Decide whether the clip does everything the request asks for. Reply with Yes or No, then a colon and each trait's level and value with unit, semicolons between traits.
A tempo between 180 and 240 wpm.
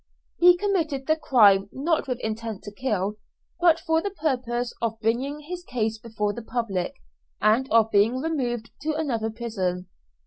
No: average, 160 wpm